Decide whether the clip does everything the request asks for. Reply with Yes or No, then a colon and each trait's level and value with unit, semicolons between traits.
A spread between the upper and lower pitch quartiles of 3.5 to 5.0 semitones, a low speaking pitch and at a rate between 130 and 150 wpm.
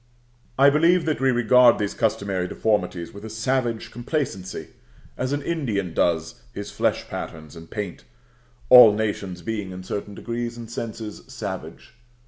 Yes: average, 4.6 semitones; low, 110 Hz; average, 145 wpm